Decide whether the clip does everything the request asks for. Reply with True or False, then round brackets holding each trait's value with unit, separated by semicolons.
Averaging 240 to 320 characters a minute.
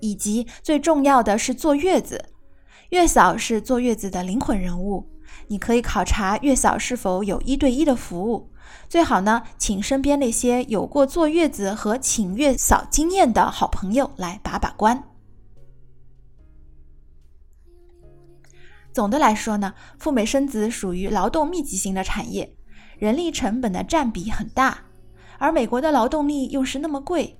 False (230 characters per minute)